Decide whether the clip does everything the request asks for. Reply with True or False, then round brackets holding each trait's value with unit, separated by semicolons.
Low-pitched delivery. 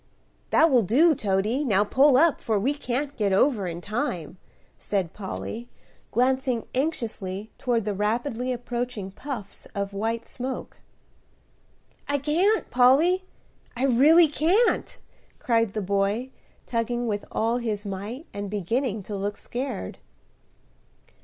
False (235 Hz)